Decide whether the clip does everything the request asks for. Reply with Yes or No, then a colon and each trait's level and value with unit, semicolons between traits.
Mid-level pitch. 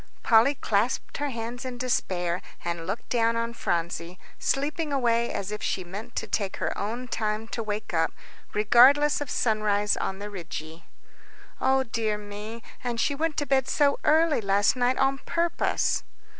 No: high, 230 Hz